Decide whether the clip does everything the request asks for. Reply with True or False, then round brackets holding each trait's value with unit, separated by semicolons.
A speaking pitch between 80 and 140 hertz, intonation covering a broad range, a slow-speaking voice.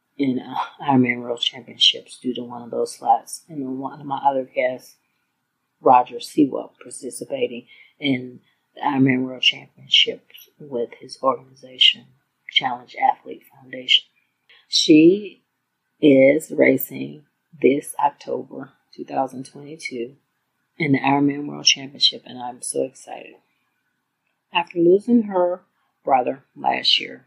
True (135 Hz; 5.9 semitones; 110 wpm)